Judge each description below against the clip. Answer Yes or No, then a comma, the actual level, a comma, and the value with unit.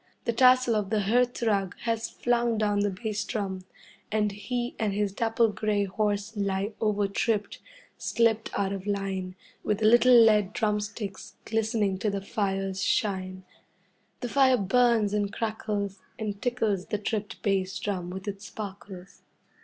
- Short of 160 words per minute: Yes, average, 150 wpm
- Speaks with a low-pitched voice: No, high, 210 Hz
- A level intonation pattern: Yes, narrow, 2.3 semitones